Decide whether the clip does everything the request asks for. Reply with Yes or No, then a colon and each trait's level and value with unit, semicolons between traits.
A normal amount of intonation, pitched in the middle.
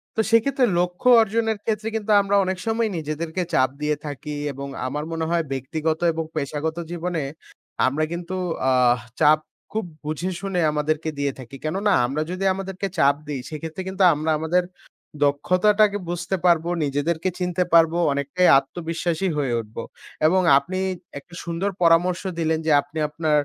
Yes: average, 3.8 semitones; medium, 165 Hz